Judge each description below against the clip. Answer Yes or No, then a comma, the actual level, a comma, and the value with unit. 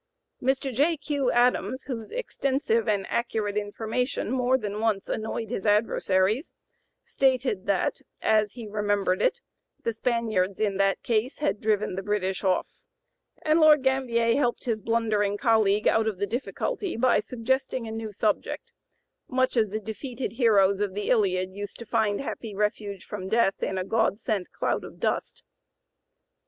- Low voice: No, high, 220 Hz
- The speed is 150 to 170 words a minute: Yes, average, 160 wpm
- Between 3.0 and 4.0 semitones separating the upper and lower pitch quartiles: Yes, average, 3.4 semitones